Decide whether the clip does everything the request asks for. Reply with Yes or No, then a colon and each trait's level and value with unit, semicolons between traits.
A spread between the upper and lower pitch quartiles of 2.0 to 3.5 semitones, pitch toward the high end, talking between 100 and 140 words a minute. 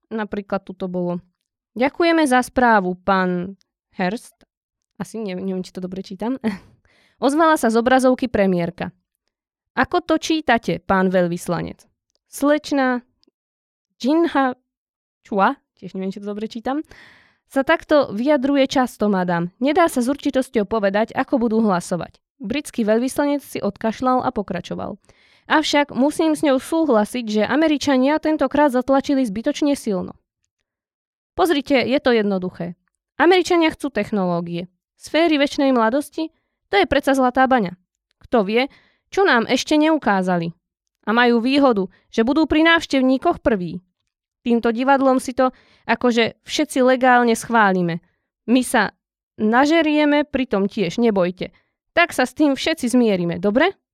No: wide, 6.2 semitones; very high, 250 Hz; average, 130 wpm